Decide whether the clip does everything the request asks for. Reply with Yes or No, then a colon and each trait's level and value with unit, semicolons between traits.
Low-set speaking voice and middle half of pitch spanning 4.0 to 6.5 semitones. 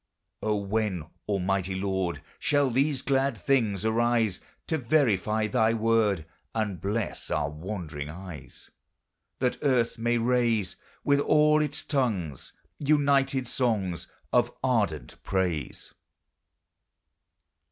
Yes: low, 110 Hz; wide, 5.4 semitones